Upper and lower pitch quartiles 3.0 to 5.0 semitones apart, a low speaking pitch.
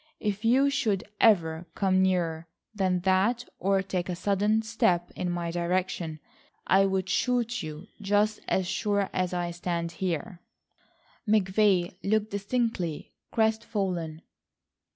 No: average, 3.4 semitones; high, 190 Hz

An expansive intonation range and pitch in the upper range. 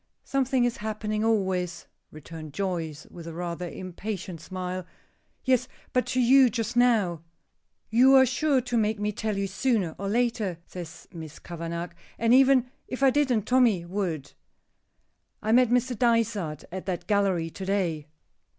Yes: wide, 5.7 semitones; high, 205 Hz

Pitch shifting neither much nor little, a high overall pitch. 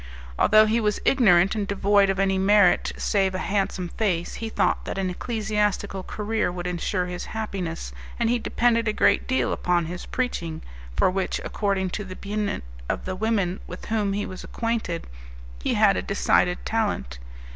Yes: average, 3.0 semitones; high, 195 Hz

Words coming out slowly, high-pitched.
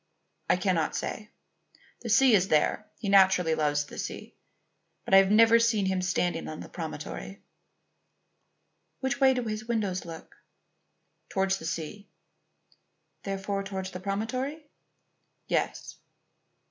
Yes: slow, 130 wpm; high, 195 Hz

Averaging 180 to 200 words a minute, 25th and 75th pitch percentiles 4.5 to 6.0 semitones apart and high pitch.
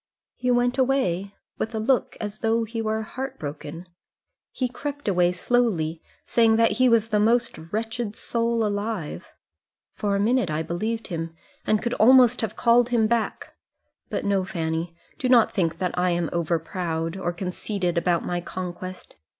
No: average, 165 wpm; average, 5.0 semitones; high, 210 Hz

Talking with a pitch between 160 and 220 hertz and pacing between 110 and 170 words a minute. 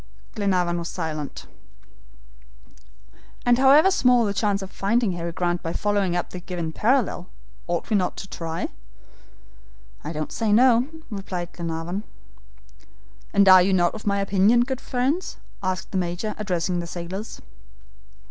Yes: high, 190 Hz; average, 145 wpm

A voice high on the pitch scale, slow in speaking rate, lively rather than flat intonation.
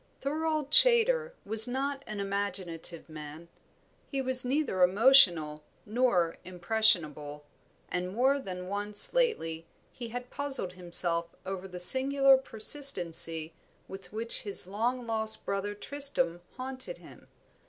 Yes: high, 210 Hz; slow, 120 wpm; wide, 7.0 semitones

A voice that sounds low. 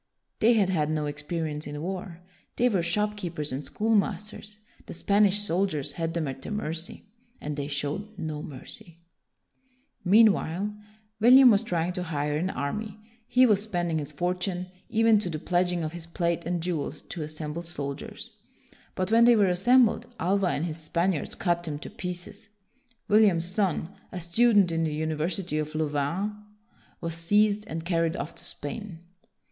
No: medium, 175 Hz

